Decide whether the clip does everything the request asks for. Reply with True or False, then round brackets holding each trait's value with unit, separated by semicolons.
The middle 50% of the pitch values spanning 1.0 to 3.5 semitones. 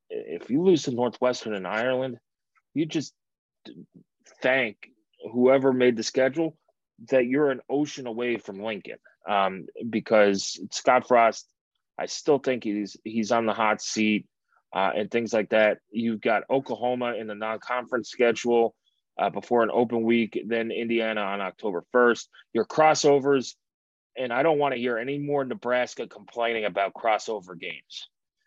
True (3.2 semitones)